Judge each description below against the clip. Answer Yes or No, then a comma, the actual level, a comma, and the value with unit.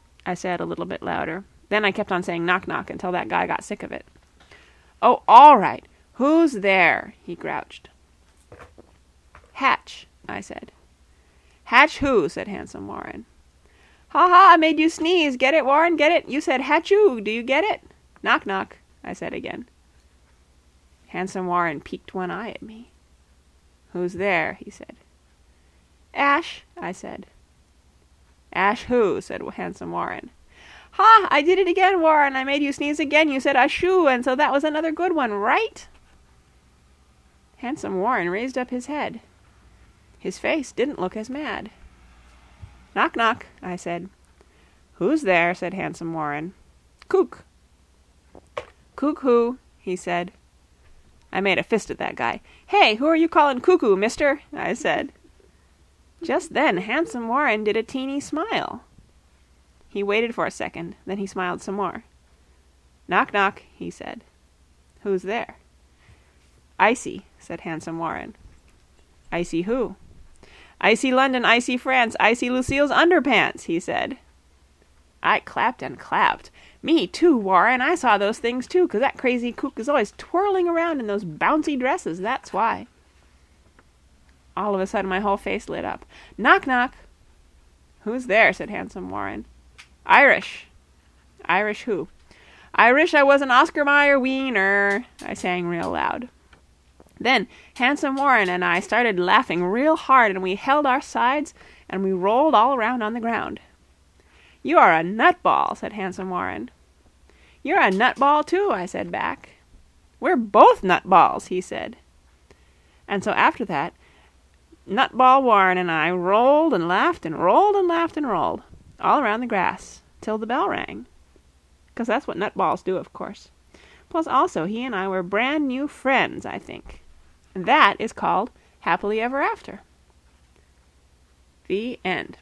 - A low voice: No, high, 190 Hz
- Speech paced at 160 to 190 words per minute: No, average, 150 wpm